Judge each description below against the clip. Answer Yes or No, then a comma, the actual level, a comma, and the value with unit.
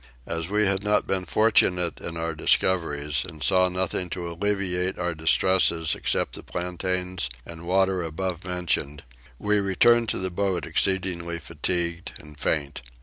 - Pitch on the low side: Yes, very low, 90 Hz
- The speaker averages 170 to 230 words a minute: No, average, 145 wpm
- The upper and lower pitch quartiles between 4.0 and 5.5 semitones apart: No, narrow, 2.4 semitones